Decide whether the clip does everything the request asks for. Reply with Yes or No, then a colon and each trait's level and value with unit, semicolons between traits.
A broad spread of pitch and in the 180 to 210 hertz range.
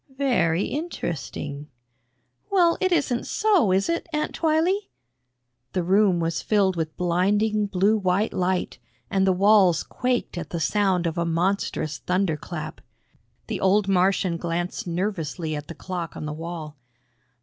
No: average, 4.1 semitones; medium, 185 Hz